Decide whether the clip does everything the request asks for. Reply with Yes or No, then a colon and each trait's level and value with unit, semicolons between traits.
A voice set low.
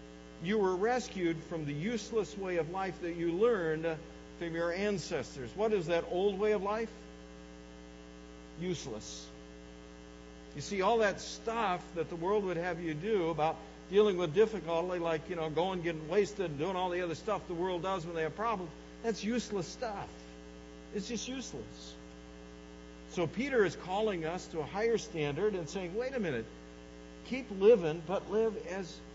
No: medium, 170 Hz